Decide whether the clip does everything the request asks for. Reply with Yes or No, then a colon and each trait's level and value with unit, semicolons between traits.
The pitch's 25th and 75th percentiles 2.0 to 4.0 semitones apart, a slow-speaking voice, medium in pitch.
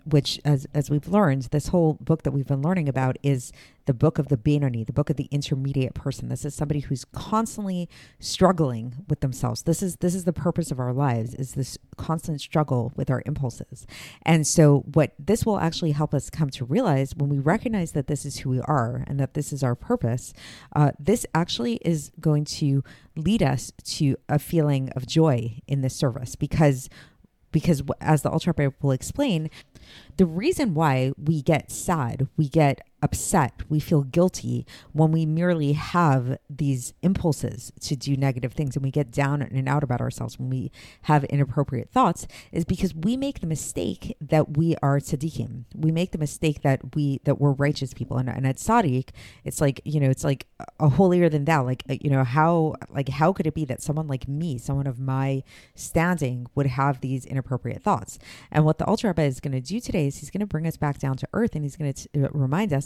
No: average, 3.1 semitones; fast, 205 wpm; medium, 145 Hz